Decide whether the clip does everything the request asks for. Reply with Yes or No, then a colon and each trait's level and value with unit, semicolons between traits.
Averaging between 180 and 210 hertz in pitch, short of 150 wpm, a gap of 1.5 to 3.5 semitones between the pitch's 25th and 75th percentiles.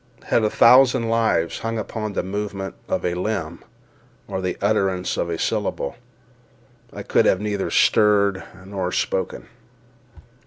No: low, 100 Hz; average, 140 wpm; average, 2.9 semitones